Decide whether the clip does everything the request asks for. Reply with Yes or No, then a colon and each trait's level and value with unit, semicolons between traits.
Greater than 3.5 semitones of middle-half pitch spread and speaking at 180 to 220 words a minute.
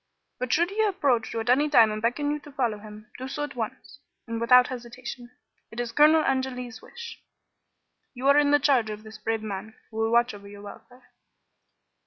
Yes: average, 4.1 semitones; fast, 205 wpm